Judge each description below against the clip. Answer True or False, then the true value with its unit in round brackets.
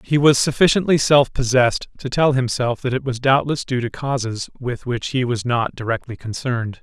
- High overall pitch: False (125 Hz)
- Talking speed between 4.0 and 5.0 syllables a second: False (5.2 syllables/s)